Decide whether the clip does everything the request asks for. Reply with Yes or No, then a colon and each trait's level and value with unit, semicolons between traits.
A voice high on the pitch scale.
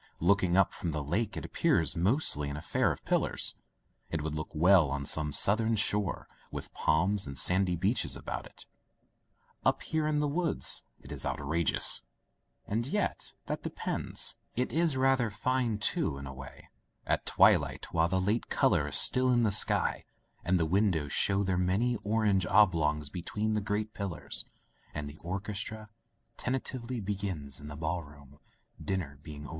No: very low, 95 Hz